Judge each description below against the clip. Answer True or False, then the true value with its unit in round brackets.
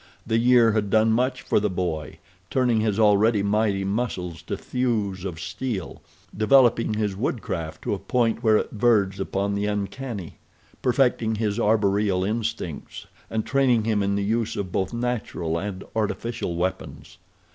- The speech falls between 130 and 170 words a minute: True (150 wpm)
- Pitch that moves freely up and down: False (3.0 semitones)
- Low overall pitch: True (105 Hz)